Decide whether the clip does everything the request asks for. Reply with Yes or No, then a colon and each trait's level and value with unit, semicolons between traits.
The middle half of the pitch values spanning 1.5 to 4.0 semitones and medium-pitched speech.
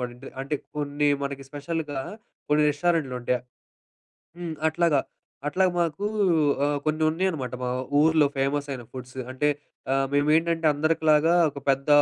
Yes: average, 2.9 semitones; medium, 150 Hz